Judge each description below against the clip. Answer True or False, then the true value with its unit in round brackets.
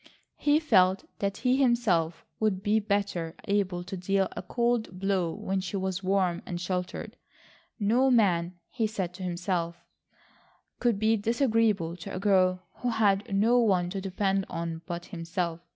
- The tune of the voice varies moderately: True (3.3 semitones)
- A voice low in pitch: False (195 Hz)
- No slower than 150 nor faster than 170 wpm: True (155 wpm)